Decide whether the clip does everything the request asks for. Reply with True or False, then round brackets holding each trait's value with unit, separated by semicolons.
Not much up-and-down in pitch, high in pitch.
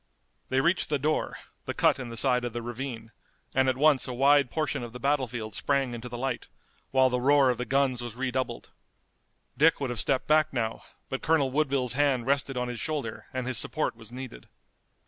False (2.3 semitones; 130 Hz)